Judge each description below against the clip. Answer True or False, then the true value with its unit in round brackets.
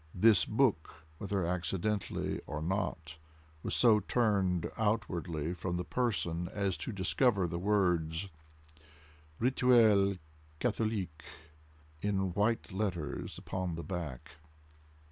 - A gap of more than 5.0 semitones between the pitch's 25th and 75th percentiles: False (3.7 semitones)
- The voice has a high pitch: False (95 Hz)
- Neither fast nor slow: False (105 wpm)